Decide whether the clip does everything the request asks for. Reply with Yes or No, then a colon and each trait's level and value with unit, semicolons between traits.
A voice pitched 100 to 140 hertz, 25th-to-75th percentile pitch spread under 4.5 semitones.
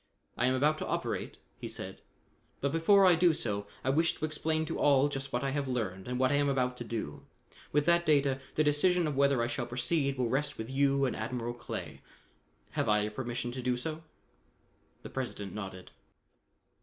Yes: low, 135 Hz; average, 3.5 semitones